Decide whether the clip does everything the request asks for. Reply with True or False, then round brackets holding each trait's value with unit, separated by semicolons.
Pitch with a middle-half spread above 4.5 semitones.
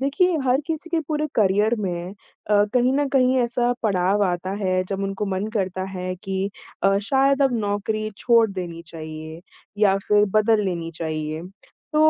True (5.1 semitones)